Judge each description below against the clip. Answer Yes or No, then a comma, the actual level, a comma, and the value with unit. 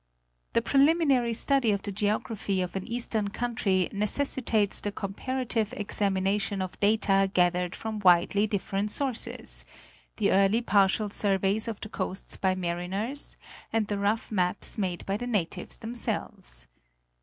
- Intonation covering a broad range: No, average, 2.8 semitones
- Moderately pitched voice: No, high, 205 Hz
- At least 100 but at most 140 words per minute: Yes, slow, 135 wpm